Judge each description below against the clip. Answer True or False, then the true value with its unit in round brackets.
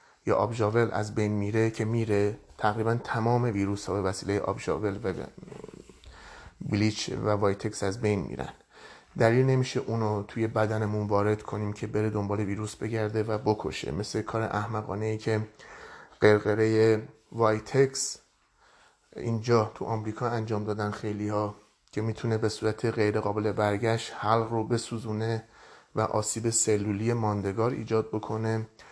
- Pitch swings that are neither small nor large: False (1.3 semitones)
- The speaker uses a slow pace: False (135 wpm)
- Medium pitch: False (110 Hz)